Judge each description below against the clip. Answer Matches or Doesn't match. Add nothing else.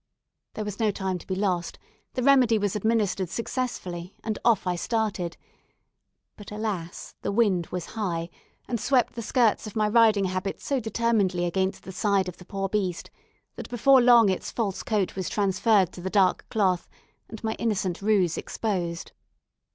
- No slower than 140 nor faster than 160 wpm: Doesn't match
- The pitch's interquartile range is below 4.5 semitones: Matches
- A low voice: Doesn't match